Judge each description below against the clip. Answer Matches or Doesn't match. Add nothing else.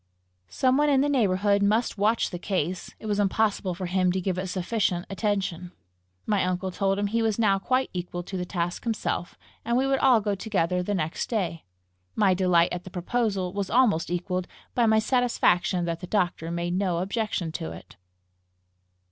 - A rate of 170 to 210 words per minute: Matches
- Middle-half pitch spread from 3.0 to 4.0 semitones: Matches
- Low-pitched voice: Doesn't match